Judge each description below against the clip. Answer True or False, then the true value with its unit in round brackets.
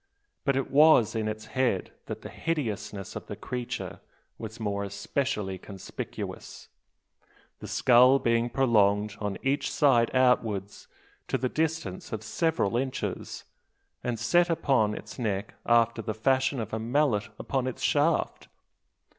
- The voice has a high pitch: False (115 Hz)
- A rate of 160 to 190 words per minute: False (140 wpm)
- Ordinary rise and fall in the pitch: True (4.1 semitones)